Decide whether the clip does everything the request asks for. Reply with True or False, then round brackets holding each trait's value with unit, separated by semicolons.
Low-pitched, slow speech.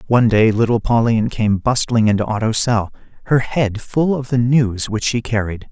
False (115 Hz; 190 wpm)